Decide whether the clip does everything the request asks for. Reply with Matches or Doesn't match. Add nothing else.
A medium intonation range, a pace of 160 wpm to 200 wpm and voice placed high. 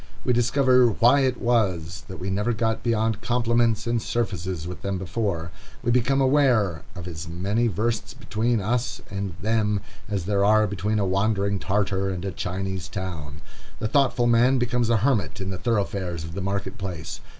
Doesn't match